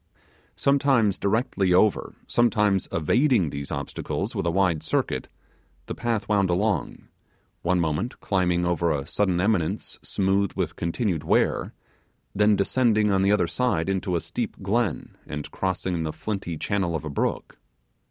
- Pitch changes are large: No, average, 3.8 semitones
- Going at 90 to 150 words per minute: Yes, average, 145 wpm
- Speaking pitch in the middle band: No, very low, 95 Hz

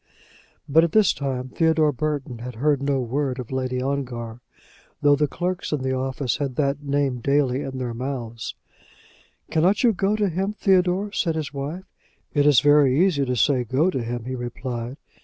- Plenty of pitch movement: No, average, 3.6 semitones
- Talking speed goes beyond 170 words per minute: Yes, average, 180 wpm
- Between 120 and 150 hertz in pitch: Yes, medium, 140 Hz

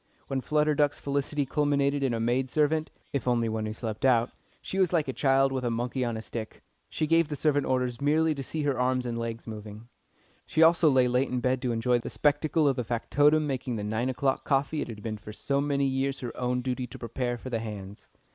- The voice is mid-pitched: No, low, 130 Hz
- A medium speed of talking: No, fast, 235 wpm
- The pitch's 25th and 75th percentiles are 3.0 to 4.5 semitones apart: Yes, average, 3.5 semitones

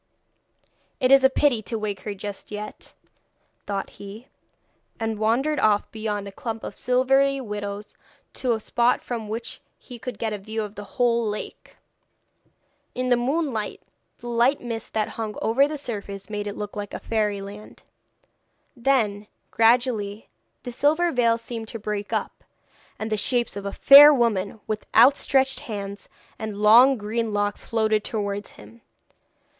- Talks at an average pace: Yes, average, 150 wpm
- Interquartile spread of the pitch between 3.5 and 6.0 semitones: No, average, 3.0 semitones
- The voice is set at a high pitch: Yes, high, 220 Hz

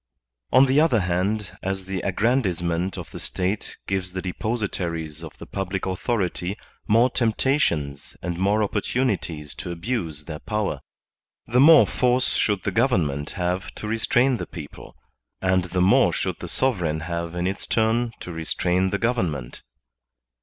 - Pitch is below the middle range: Yes, very low, 95 Hz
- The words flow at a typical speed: Yes, average, 155 wpm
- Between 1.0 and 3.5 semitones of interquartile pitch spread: No, average, 4.6 semitones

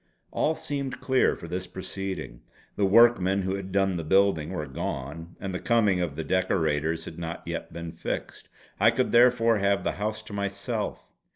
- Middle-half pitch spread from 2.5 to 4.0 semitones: No, average, 4.4 semitones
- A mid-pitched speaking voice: No, very low, 95 Hz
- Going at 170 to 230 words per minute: Yes, average, 180 wpm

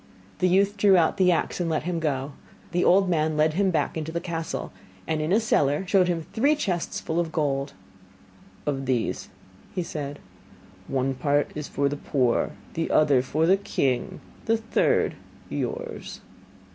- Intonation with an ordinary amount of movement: Yes, average, 4.2 semitones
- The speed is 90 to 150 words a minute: No, average, 170 wpm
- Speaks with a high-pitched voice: No, medium, 160 Hz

